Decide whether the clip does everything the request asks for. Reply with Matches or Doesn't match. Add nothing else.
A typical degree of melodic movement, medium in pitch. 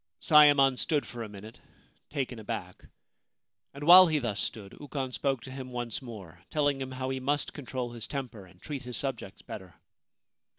Doesn't match